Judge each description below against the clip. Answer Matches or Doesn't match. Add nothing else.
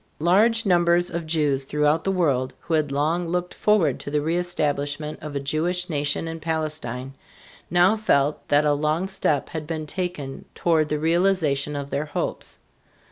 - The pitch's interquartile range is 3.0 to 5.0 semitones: Matches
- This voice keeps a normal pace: Matches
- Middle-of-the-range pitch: Matches